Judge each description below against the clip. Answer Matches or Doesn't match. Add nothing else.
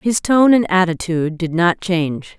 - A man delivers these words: Doesn't match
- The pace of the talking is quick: Doesn't match